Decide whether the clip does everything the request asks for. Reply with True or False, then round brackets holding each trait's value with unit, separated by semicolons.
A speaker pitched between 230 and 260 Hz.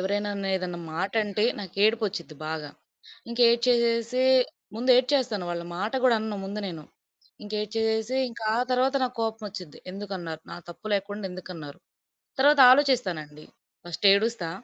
False (210 Hz)